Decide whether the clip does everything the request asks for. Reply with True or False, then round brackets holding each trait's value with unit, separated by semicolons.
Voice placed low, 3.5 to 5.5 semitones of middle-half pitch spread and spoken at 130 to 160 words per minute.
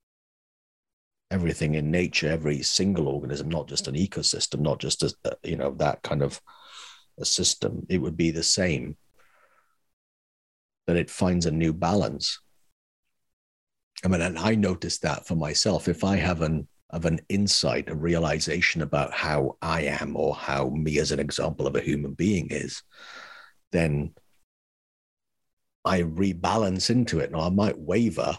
True (85 Hz; 3.8 semitones; 150 wpm)